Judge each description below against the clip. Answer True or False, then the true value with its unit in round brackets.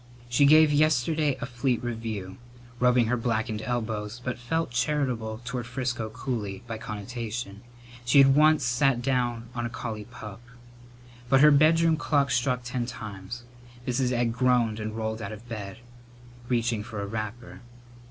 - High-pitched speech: False (120 Hz)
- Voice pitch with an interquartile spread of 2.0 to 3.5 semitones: True (2.7 semitones)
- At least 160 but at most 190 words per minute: False (150 wpm)